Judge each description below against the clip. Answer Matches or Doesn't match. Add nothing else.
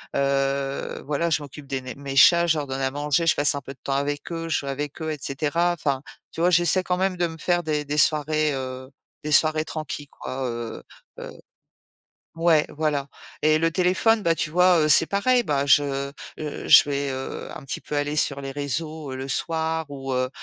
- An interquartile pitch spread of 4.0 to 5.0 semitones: Doesn't match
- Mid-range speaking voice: Matches